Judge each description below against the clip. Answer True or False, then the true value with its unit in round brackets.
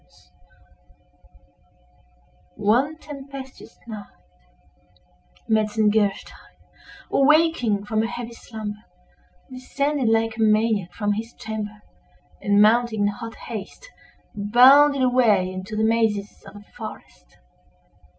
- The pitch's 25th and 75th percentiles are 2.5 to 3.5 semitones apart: True (3.1 semitones)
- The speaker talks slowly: True (95 wpm)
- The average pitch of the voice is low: False (220 Hz)